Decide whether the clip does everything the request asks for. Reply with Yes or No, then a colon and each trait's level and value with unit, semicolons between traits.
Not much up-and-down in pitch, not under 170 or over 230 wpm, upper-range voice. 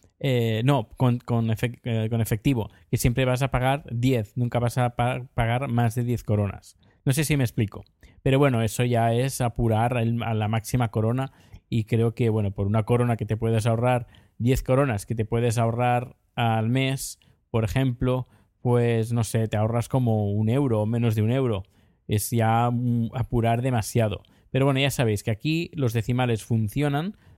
No: narrow, 2.2 semitones; average, 180 wpm; low, 120 Hz